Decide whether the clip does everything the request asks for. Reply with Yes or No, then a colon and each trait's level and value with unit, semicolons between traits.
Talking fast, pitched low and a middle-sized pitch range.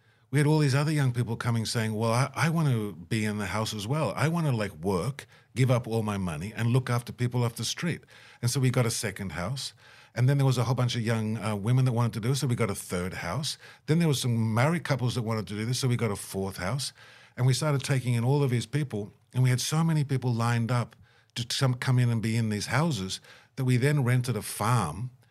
Yes: fast, 270 wpm; low, 120 Hz; average, 3.0 semitones